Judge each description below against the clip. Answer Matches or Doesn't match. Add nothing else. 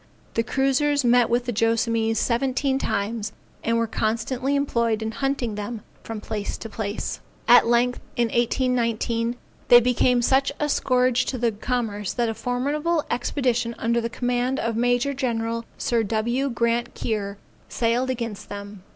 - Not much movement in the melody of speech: Matches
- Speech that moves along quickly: Doesn't match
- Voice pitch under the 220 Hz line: Doesn't match